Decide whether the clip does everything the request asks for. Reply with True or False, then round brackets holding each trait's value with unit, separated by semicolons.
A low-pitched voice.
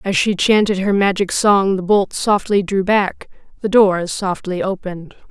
False (195 Hz)